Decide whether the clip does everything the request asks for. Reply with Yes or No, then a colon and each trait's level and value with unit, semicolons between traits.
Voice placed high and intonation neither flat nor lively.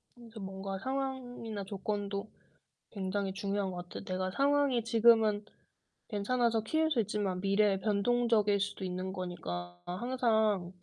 Yes: high, 205 Hz; average, 3.4 semitones